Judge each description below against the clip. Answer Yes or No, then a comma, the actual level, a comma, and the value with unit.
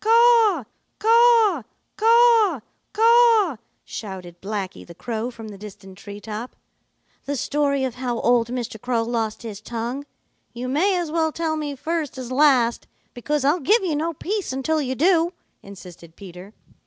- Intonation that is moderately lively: No, wide, 7.3 semitones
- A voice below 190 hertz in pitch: No, very high, 265 Hz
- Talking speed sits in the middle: Yes, average, 155 wpm